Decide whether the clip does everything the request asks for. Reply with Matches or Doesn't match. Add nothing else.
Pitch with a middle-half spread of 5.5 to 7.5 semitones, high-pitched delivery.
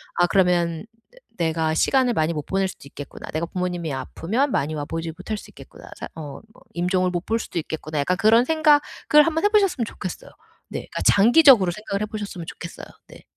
Doesn't match